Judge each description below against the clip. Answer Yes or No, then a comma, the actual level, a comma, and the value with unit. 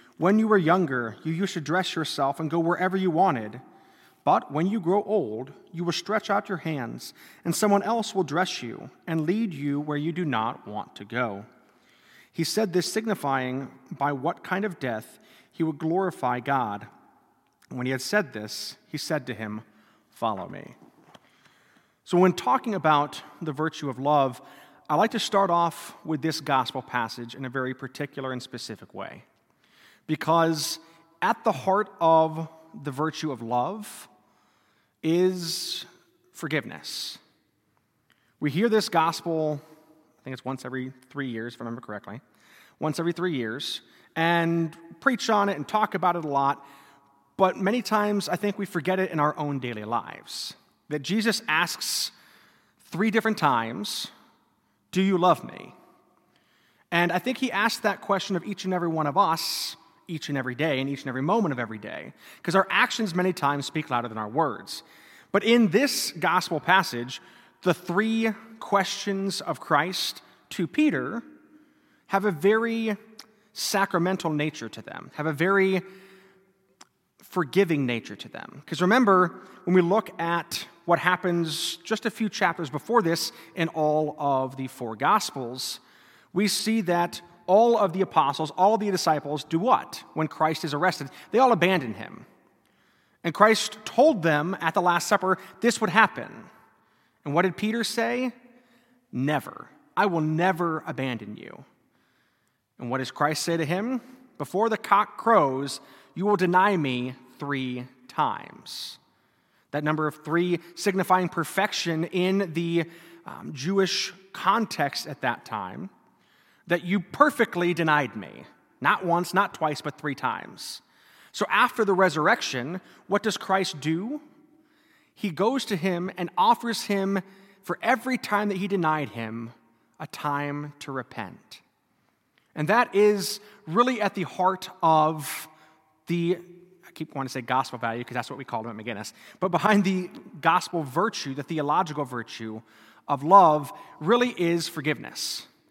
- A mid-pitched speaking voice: Yes, medium, 170 Hz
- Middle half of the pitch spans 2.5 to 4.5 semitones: No, wide, 5.4 semitones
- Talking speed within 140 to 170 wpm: Yes, average, 160 wpm